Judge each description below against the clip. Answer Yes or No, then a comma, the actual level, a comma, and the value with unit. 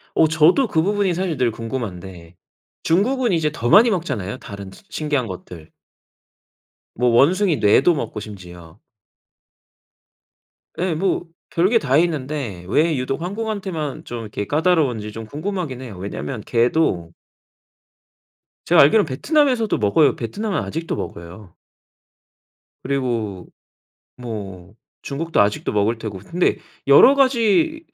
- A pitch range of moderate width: No, wide, 8.9 semitones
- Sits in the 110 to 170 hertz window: Yes, medium, 140 Hz